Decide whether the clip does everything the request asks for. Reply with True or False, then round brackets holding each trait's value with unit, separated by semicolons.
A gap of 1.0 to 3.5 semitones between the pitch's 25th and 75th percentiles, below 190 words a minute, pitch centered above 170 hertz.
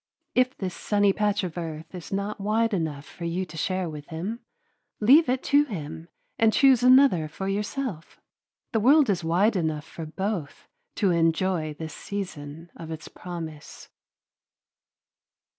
False (4.8 semitones; 150 wpm; 185 Hz)